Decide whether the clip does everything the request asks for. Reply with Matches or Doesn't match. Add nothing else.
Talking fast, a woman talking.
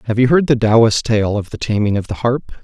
Doesn't match